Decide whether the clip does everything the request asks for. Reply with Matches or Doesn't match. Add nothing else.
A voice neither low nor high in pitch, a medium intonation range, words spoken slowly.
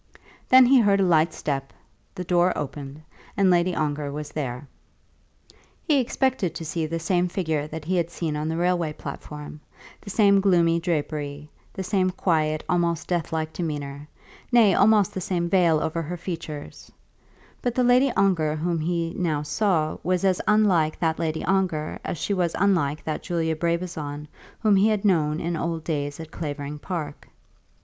Doesn't match